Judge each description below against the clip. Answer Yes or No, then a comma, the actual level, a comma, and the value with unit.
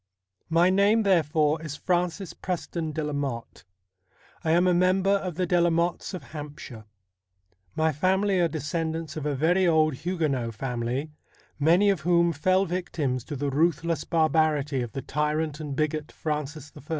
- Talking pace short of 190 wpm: Yes, average, 160 wpm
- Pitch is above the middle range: No, medium, 160 Hz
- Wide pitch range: No, average, 3.1 semitones